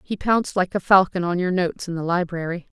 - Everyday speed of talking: No, fast, 235 wpm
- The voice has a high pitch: No, medium, 180 Hz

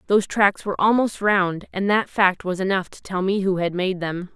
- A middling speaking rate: No, fast, 235 wpm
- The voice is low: No, high, 190 Hz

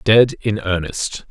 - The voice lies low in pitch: Yes, low, 105 Hz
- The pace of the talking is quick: No, average, 140 wpm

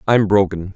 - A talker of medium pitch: No, low, 100 Hz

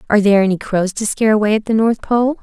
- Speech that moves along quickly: Yes, fast, 270 wpm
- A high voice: Yes, high, 215 Hz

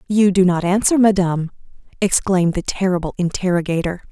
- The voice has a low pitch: No, medium, 185 Hz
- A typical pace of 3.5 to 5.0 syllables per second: No, 6.0 syllables/s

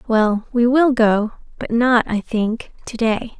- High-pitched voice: Yes, high, 230 Hz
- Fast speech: No, average, 175 wpm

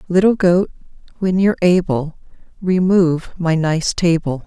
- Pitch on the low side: No, medium, 175 Hz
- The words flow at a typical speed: No, slow, 120 wpm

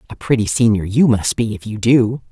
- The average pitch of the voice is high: No, low, 115 Hz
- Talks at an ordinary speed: No, fast, 235 wpm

